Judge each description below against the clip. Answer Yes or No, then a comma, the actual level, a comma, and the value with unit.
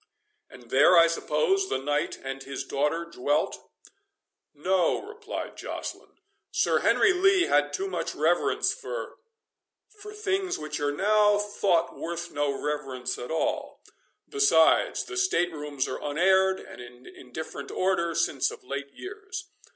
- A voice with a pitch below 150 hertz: No, medium, 170 Hz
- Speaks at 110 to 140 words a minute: Yes, slow, 135 wpm